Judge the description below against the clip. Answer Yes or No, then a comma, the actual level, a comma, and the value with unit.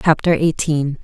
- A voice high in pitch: No, medium, 155 Hz